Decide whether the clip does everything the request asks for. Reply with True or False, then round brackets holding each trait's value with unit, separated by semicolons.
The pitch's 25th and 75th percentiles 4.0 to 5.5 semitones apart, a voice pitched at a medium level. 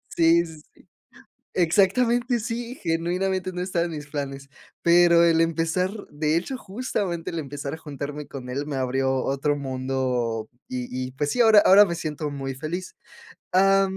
True (5.0 semitones; 165 Hz)